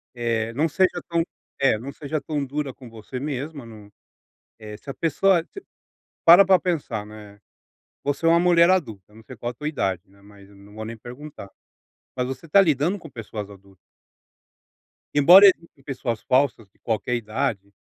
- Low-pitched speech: Yes, low, 130 Hz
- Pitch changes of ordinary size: No, wide, 6.4 semitones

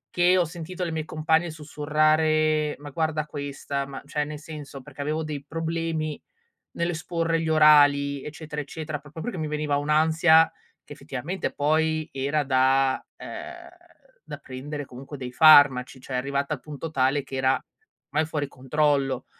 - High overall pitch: No, medium, 150 Hz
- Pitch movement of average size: No, narrow, 2.1 semitones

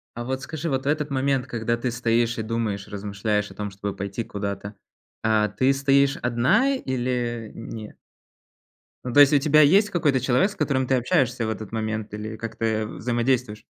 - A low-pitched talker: Yes, low, 120 Hz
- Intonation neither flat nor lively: Yes, average, 3.7 semitones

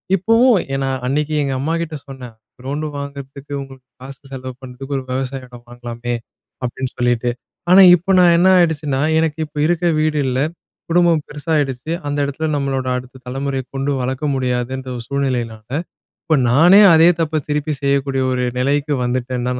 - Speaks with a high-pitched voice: No, low, 135 Hz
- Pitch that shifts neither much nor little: Yes, average, 3.2 semitones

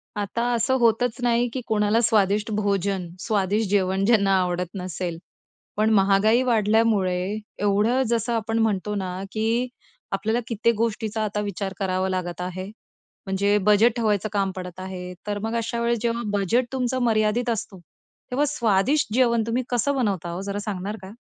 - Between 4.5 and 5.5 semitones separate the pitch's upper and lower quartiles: No, average, 3.2 semitones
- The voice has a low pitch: No, high, 210 Hz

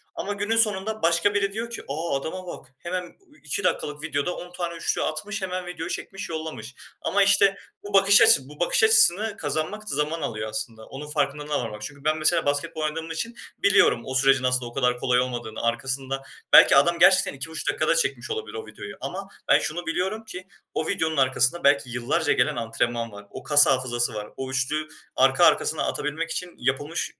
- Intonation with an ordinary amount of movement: No, wide, 5.9 semitones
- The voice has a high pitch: No, medium, 155 Hz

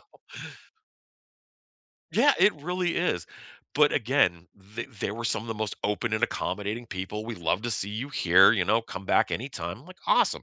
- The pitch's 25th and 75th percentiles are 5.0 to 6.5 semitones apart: Yes, wide, 5.6 semitones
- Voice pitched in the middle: No, low, 110 Hz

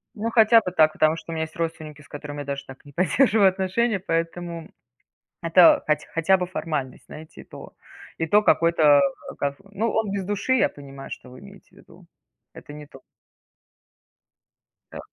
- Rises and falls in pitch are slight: No, average, 4.5 semitones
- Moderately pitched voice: Yes, medium, 165 Hz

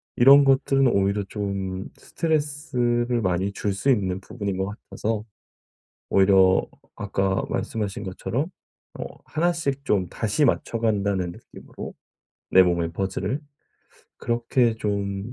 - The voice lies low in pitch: Yes, low, 105 Hz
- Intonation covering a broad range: No, average, 4.3 semitones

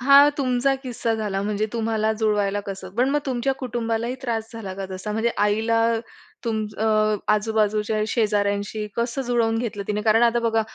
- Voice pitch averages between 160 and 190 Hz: No, high, 225 Hz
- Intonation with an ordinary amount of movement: No, narrow, 2.1 semitones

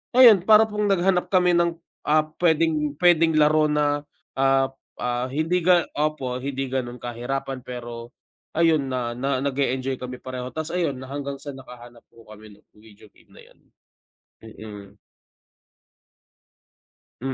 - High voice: No, low, 135 Hz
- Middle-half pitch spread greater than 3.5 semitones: Yes, average, 4.3 semitones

